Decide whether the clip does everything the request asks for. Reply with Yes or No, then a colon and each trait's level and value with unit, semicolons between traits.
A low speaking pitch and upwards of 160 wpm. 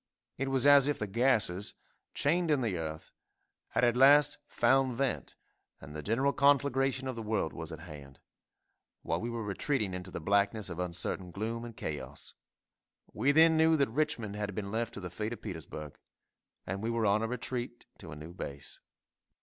Yes: low, 110 Hz; average, 185 wpm